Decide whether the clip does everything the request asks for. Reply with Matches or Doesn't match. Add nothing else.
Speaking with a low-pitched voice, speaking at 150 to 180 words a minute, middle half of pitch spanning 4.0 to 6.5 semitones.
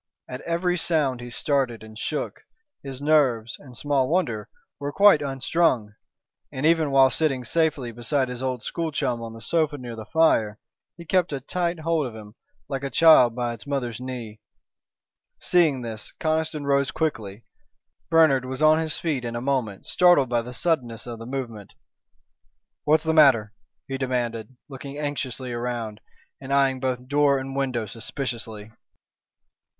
Matches